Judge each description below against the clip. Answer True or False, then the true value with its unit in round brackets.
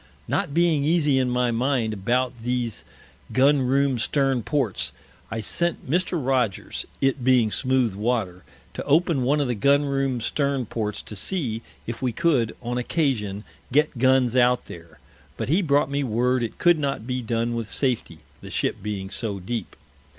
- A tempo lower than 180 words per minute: True (170 wpm)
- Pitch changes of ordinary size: True (3.6 semitones)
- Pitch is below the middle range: True (125 Hz)